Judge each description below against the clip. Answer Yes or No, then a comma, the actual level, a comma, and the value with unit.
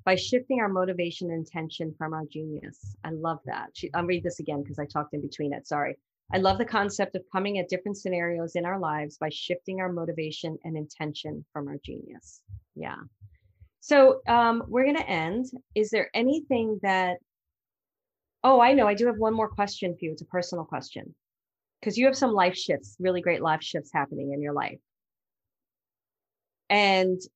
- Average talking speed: Yes, average, 185 wpm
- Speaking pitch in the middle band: Yes, medium, 180 Hz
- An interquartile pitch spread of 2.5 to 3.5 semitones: No, average, 4.9 semitones